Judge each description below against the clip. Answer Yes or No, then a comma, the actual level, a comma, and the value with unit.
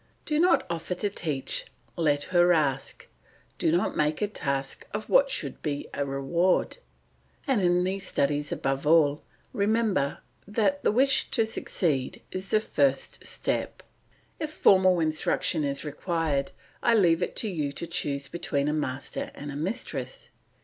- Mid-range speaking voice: Yes, medium, 165 Hz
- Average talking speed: Yes, average, 155 wpm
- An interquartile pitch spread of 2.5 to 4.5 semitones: No, wide, 5.5 semitones